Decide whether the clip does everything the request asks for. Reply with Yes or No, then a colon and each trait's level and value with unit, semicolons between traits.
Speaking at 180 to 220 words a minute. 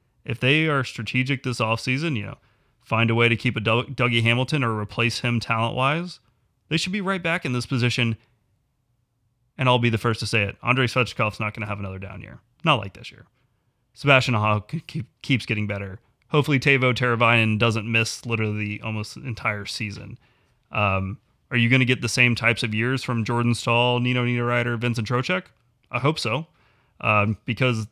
Yes: average, 190 wpm